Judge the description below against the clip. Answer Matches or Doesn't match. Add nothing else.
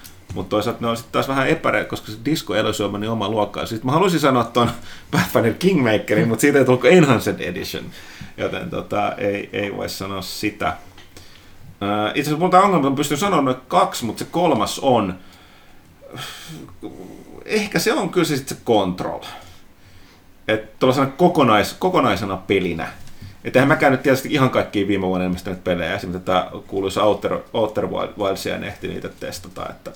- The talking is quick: Matches